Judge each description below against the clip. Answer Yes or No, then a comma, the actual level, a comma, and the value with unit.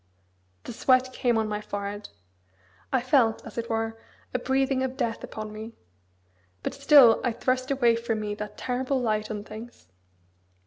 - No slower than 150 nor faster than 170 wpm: Yes, average, 165 wpm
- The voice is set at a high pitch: Yes, high, 230 Hz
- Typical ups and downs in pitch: Yes, average, 3.1 semitones